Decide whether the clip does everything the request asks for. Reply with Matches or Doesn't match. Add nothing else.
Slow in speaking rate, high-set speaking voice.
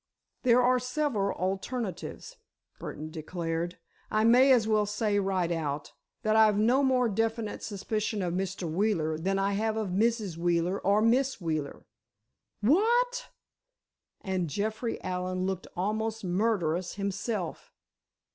Matches